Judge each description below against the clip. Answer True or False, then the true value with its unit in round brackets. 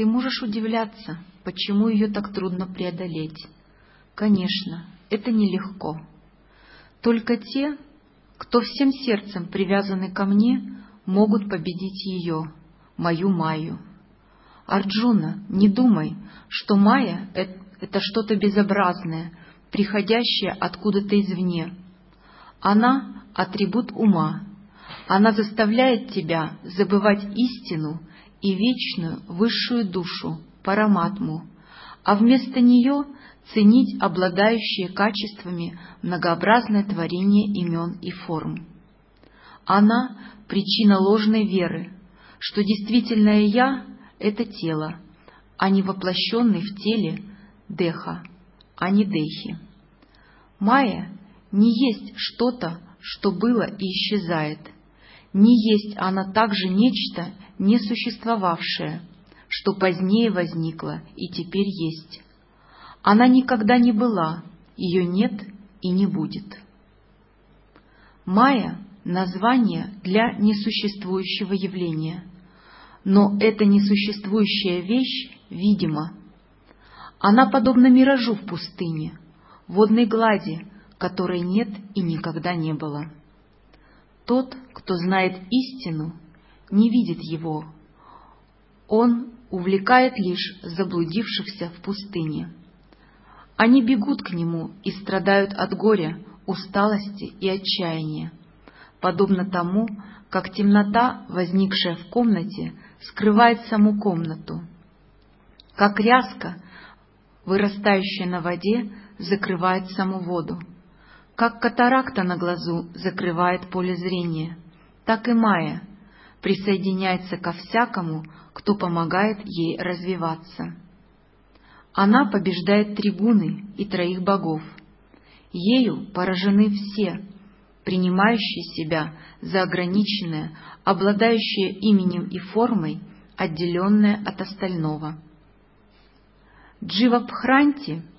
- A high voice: True (195 Hz)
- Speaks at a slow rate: True (90 wpm)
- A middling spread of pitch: True (3.3 semitones)